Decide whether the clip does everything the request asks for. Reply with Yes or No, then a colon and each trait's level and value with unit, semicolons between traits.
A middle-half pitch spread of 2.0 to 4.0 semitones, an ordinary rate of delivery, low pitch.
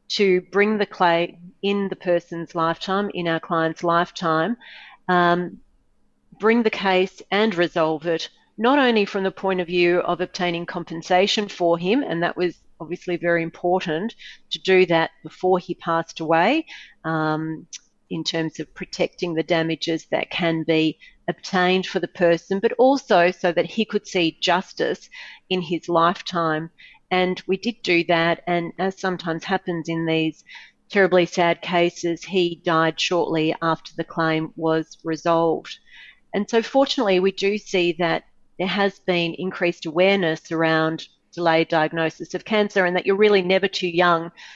No: narrow, 2.6 semitones; average, 155 wpm; medium, 175 Hz